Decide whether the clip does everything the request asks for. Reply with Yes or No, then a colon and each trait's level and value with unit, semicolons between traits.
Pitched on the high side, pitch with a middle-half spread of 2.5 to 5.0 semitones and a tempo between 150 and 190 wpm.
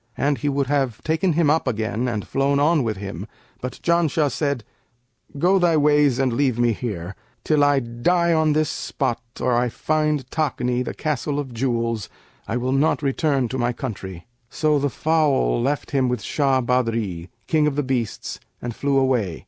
No: low, 135 Hz; average, 3.9 semitones; average, 180 wpm